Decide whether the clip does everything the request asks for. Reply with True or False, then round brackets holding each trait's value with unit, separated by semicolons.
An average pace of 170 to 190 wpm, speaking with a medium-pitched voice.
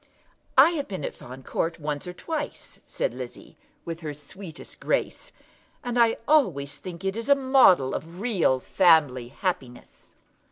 False (150 wpm; 180 Hz)